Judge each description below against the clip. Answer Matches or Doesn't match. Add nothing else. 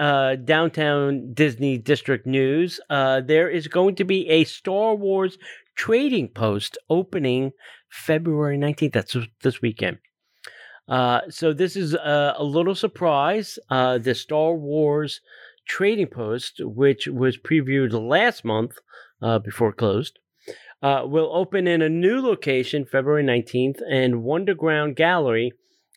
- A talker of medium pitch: Matches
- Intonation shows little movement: Doesn't match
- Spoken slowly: Matches